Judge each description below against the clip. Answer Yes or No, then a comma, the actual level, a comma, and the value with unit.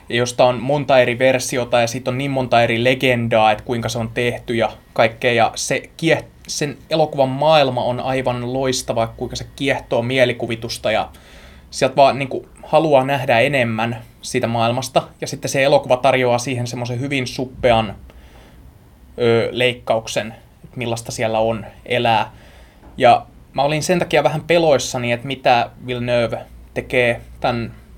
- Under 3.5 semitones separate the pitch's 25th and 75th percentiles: Yes, narrow, 2.6 semitones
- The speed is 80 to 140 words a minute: No, average, 150 wpm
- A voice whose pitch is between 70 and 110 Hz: No, low, 125 Hz